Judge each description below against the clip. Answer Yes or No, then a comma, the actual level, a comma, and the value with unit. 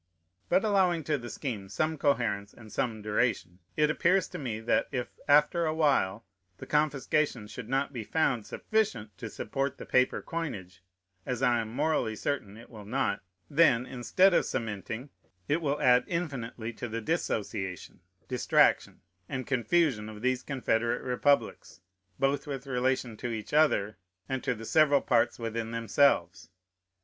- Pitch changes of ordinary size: Yes, average, 4.9 semitones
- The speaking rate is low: No, average, 155 wpm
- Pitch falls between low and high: No, low, 125 Hz